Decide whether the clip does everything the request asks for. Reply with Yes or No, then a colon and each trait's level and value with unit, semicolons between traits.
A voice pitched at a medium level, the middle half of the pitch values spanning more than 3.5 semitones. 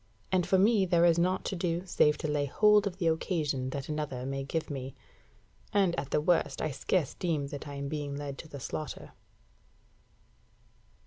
Yes: medium, 155 Hz; average, 4.0 semitones